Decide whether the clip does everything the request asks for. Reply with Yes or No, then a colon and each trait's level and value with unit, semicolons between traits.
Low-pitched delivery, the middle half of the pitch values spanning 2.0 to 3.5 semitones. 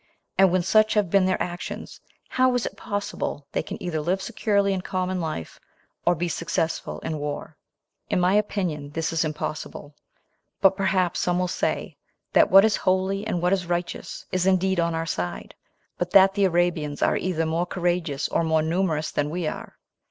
No: medium, 180 Hz; average, 2.9 semitones